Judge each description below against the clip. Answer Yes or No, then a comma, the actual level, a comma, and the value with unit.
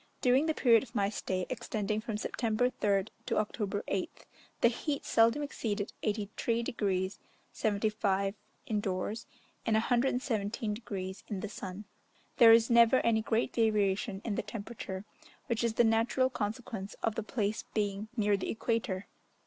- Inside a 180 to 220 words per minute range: No, average, 150 wpm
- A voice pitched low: No, high, 215 Hz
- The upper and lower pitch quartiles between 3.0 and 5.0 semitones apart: No, narrow, 2.4 semitones